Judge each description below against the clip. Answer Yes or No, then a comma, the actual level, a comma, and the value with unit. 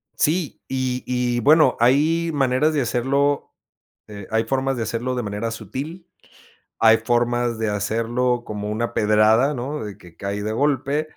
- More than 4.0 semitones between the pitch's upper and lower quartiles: No, average, 3.7 semitones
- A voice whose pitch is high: No, low, 120 Hz